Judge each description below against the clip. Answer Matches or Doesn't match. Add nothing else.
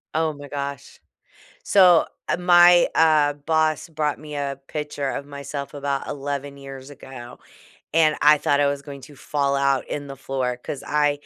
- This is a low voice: Doesn't match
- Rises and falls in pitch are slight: Matches